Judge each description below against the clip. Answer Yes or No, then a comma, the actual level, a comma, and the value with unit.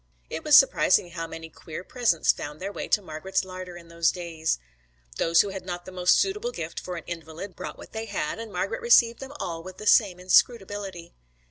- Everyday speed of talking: No, fast, 210 wpm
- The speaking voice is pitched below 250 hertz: Yes, medium, 185 Hz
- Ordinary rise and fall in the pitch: Yes, average, 3.6 semitones